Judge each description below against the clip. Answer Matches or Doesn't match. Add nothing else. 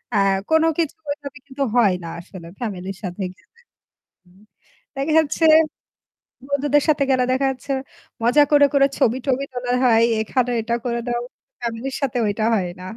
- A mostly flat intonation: Doesn't match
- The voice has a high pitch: Matches